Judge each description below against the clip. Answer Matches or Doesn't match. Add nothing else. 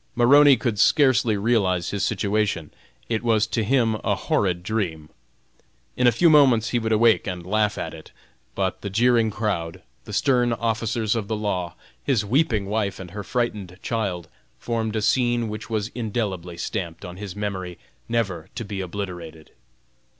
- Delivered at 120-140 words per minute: Doesn't match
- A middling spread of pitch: Matches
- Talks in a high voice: Doesn't match